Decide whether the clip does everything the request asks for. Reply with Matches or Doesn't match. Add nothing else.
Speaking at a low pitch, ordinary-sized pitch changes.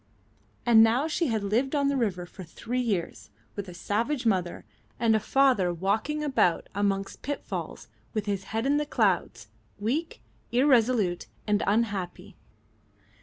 Doesn't match